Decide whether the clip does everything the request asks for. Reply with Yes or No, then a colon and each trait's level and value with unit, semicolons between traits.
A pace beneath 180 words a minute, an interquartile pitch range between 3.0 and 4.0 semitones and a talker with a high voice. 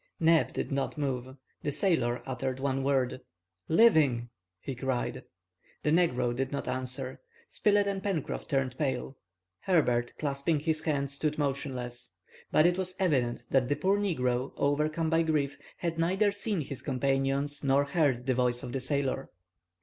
No: average, 155 wpm; average, 3.7 semitones; medium, 140 Hz